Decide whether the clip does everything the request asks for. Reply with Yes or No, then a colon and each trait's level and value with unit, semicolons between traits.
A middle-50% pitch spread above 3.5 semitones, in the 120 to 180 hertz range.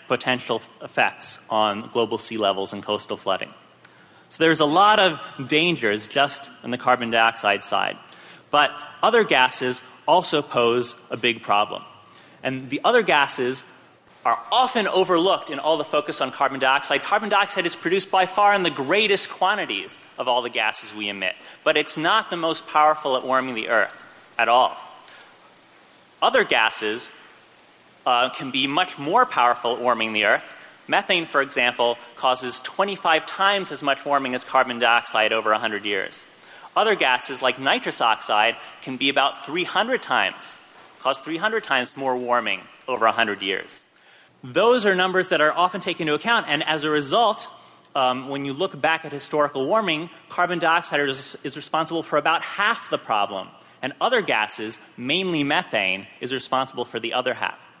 Yes: average, 5.3 semitones; medium, 140 Hz